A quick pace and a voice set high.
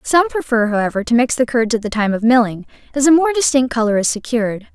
Yes: fast, 240 wpm; high, 245 Hz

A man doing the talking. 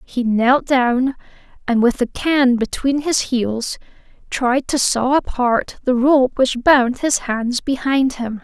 No: female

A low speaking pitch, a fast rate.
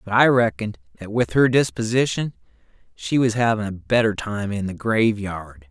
No: low, 105 Hz; average, 170 wpm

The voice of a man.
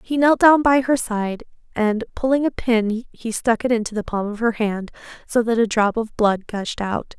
No: female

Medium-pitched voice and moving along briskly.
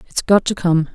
Yes: medium, 180 Hz; fast, 255 wpm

